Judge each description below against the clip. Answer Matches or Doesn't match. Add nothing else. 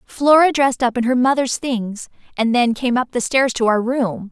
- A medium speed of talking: Doesn't match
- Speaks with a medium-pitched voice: Doesn't match